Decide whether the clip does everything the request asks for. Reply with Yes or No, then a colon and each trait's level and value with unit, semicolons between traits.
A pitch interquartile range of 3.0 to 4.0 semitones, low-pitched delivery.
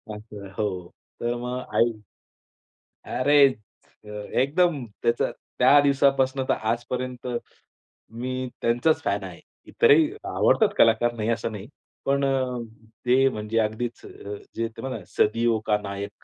Yes: average, 3.4 semitones; low, 120 Hz